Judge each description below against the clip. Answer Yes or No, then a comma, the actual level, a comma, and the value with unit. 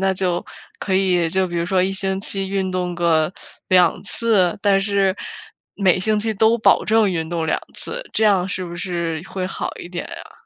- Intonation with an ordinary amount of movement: No, narrow, 2.2 semitones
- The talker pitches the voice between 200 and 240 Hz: No, high, 190 Hz